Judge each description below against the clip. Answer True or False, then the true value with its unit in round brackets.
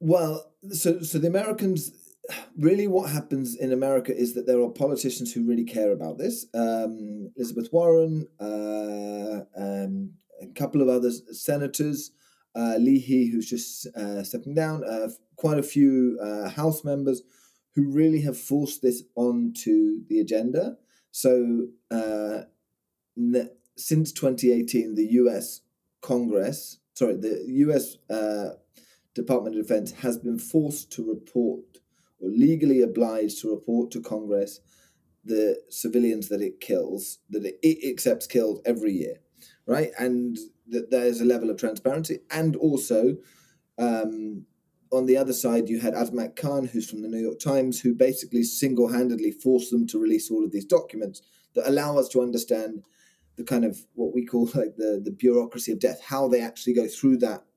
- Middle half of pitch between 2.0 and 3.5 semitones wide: False (4.1 semitones)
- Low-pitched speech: True (125 Hz)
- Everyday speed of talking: True (155 wpm)